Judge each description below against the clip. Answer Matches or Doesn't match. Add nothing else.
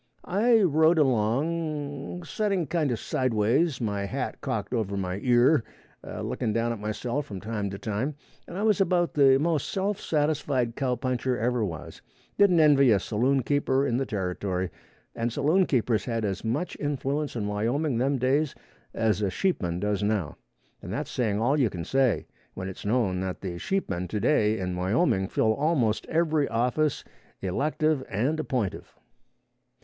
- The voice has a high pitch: Doesn't match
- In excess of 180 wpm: Doesn't match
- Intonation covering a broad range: Matches